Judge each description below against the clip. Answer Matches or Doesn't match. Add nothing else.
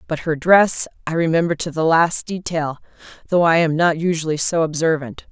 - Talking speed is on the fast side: Doesn't match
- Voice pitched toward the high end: Doesn't match